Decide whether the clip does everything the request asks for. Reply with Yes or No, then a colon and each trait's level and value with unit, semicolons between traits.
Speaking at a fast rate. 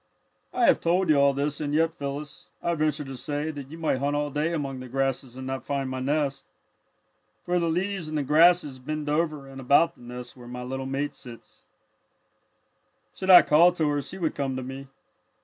Yes: fast, 210 wpm